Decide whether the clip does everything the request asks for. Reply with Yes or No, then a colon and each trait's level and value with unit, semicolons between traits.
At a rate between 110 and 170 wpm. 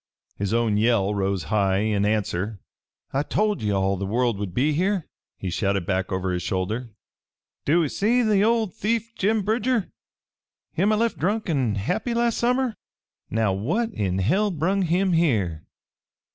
Yes: average, 160 wpm